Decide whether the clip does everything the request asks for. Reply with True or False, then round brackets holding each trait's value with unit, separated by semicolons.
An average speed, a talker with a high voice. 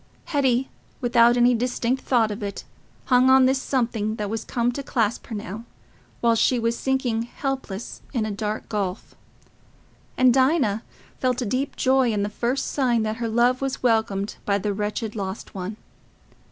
True (170 wpm; 235 Hz)